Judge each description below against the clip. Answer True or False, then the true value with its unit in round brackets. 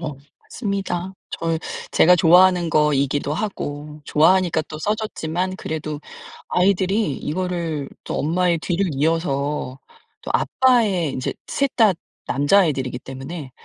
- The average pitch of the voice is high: False (165 Hz)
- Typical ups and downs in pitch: True (4.0 semitones)